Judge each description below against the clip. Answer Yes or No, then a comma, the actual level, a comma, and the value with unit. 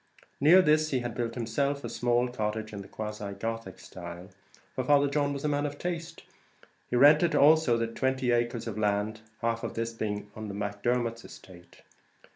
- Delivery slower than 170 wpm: No, average, 185 wpm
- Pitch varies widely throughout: No, average, 4.8 semitones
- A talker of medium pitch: No, low, 120 Hz